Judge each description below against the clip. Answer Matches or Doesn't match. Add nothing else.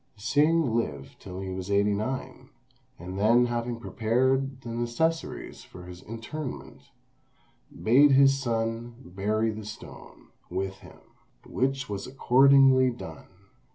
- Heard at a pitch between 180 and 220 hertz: Doesn't match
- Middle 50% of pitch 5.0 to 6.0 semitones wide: Doesn't match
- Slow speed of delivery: Matches